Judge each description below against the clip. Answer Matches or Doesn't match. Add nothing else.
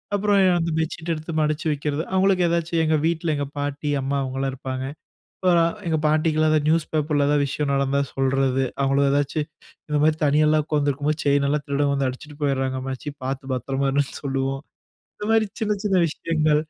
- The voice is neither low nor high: Matches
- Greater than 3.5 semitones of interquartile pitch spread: Doesn't match